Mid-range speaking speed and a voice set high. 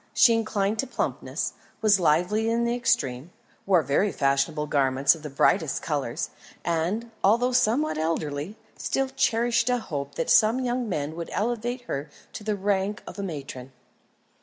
Yes: average, 160 wpm; high, 200 Hz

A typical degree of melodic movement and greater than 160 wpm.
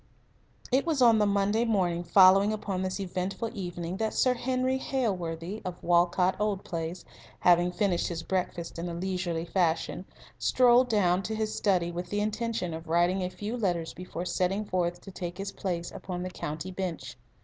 Yes: average, 3.2 semitones; average, 175 wpm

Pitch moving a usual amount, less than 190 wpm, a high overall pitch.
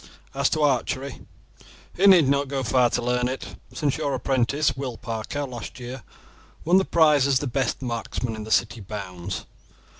No: average, 3.2 semitones; average, 175 wpm; low, 130 Hz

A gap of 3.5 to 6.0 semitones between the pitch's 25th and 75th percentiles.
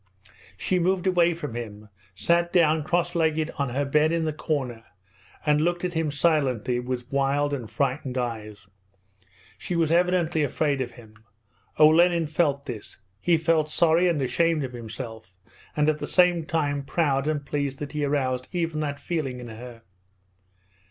Yes: average, 4.5 semitones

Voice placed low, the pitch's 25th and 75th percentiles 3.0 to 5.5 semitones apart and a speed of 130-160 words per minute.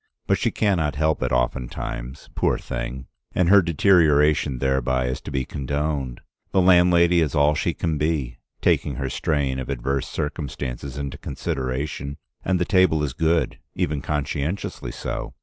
Yes: very low, 75 Hz; average, 3.8 semitones; average, 155 wpm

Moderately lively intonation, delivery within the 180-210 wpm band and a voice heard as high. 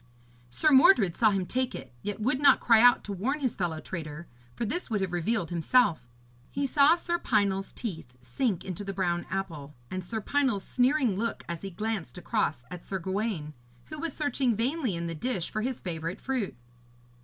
No: wide, 6.7 semitones; average, 190 wpm; high, 205 Hz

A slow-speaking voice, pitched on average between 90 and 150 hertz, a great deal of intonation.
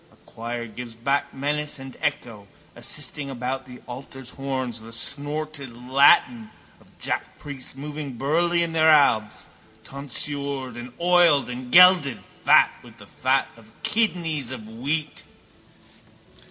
No: slow, 125 wpm; low, 135 Hz; average, 3.6 semitones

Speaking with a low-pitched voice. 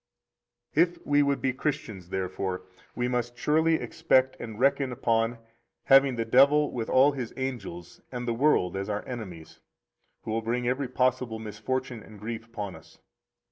Yes: low, 120 Hz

